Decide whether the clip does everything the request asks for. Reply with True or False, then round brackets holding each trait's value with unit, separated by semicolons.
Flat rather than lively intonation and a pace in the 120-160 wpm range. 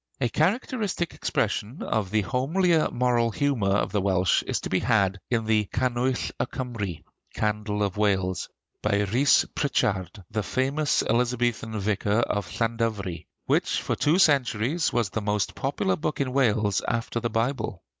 False (4.1 semitones; 155 wpm)